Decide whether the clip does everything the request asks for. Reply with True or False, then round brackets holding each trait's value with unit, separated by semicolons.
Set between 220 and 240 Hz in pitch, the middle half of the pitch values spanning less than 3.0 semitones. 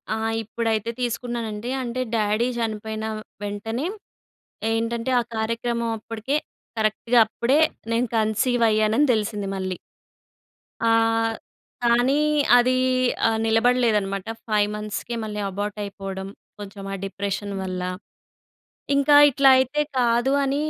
True (225 Hz; 2.5 semitones)